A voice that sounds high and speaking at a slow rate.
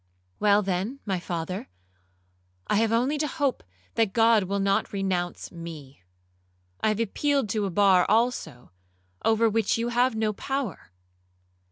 No: high, 210 Hz; average, 145 wpm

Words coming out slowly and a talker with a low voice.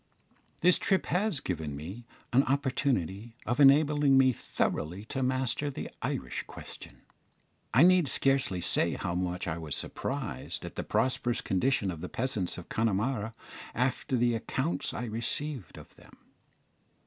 No: average, 150 wpm; low, 120 Hz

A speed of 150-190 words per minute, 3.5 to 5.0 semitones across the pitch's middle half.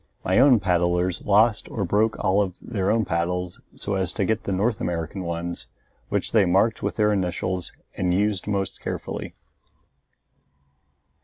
No: average, 155 wpm; average, 2.9 semitones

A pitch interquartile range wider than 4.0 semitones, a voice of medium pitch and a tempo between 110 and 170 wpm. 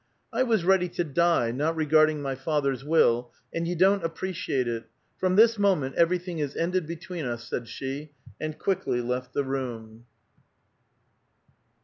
Yes: average, 5.1 semitones; medium, 155 Hz; average, 155 wpm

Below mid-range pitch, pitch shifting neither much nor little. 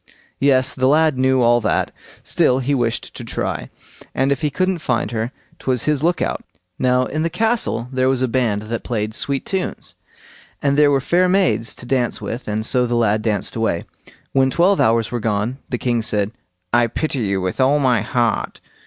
Yes: low, 125 Hz; average, 3.5 semitones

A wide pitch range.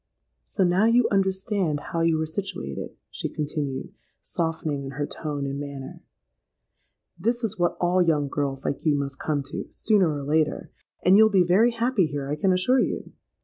No: average, 5.0 semitones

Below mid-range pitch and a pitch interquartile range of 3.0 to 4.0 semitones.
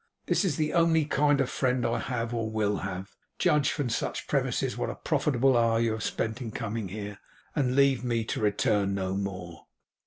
No: low, 115 Hz; average, 4.8 semitones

